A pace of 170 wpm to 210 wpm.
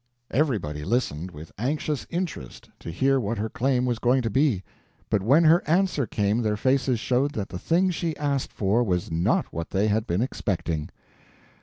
Yes: average, 180 wpm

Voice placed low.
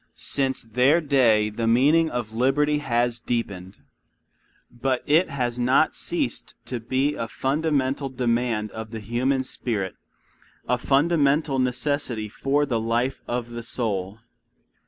Yes: low, 125 Hz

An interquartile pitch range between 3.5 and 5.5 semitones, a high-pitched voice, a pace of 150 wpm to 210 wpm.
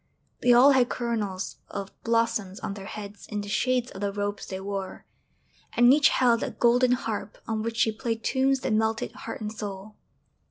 No: average, 3.0 semitones; high, 220 Hz; average, 190 wpm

